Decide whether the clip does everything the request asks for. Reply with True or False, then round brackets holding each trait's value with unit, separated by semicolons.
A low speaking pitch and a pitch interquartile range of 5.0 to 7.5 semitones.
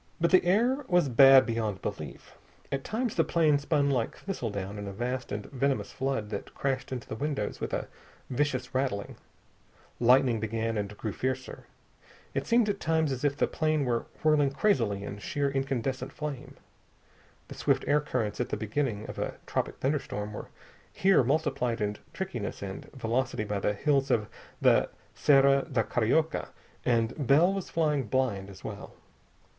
False (130 Hz; 4.6 semitones)